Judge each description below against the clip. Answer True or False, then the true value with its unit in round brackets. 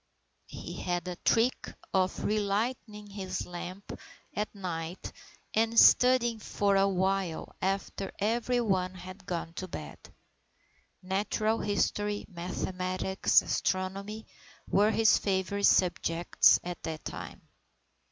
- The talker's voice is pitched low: False (195 Hz)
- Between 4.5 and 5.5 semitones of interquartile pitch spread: False (2.4 semitones)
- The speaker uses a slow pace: True (115 wpm)